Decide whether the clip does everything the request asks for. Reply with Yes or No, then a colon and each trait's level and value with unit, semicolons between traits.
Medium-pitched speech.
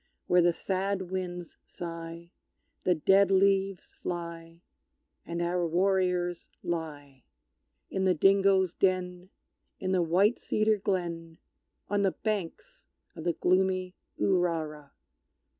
Yes: medium, 180 Hz